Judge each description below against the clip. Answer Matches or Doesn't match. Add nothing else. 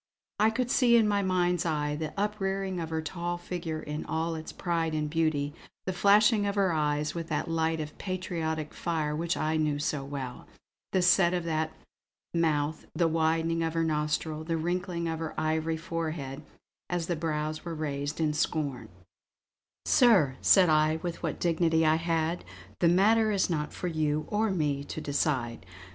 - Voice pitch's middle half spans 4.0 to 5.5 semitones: Doesn't match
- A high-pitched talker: Doesn't match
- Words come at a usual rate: Matches